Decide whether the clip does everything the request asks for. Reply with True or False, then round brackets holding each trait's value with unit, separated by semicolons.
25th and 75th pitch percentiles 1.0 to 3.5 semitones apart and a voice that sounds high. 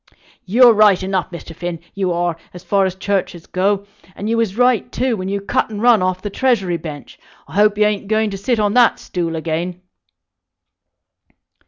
True (3.1 semitones; 195 Hz)